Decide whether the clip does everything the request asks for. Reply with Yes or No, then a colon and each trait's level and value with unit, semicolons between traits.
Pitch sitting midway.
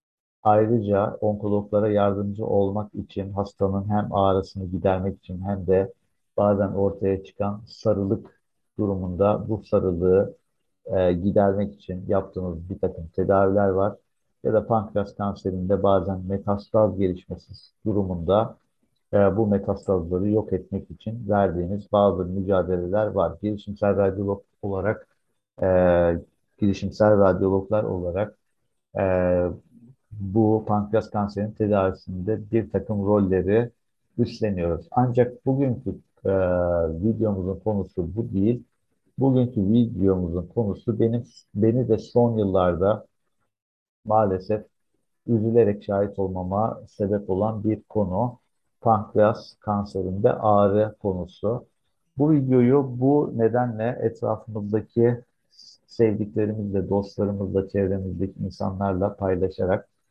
No: low, 100 Hz